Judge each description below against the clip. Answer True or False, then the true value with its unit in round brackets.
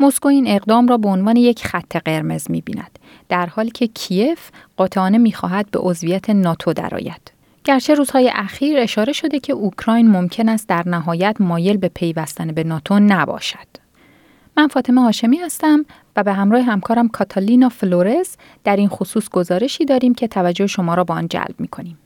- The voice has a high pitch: True (205 Hz)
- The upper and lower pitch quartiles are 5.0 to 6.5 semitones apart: True (5.4 semitones)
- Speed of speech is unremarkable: False (165 wpm)